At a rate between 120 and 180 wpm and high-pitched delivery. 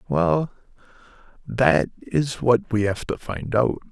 No: average, 140 wpm; low, 115 Hz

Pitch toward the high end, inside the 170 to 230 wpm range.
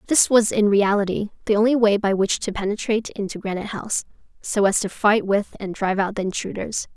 Yes: high, 205 Hz; fast, 205 wpm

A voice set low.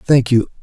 Yes: low, 125 Hz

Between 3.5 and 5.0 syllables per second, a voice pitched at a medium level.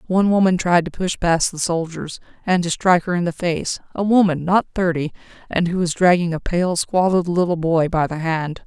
No: 5.2 syllables/s; medium, 175 Hz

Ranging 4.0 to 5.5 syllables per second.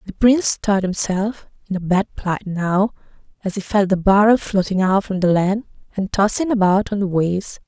Yes: 5.0 syllables/s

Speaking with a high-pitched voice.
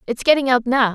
Yes: very high, 250 Hz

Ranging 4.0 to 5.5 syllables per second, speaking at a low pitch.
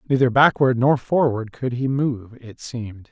Yes: 4.5 syllables/s; low, 125 Hz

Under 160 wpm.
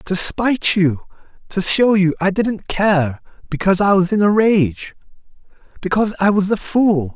Yes: average, 145 wpm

